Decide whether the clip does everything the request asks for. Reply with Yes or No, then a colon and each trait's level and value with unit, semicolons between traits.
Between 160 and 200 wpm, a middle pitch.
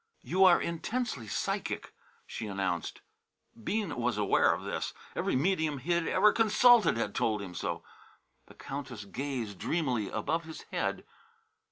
No: average, 145 wpm; medium, 145 Hz